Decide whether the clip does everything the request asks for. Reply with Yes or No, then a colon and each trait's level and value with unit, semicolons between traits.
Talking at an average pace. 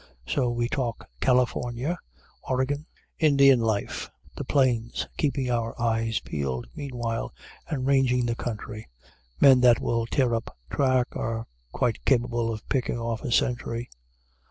No: slow, 130 wpm